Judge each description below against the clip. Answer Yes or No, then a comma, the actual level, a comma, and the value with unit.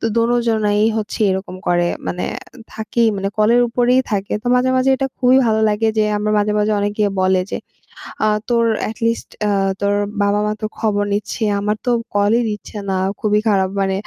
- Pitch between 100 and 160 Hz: No, high, 210 Hz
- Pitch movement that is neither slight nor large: No, narrow, 2.2 semitones